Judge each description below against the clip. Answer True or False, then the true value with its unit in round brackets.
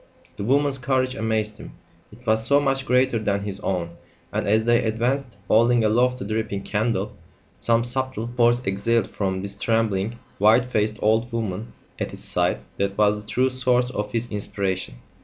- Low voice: True (110 Hz)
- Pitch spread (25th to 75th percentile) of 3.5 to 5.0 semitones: False (3.1 semitones)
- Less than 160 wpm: False (175 wpm)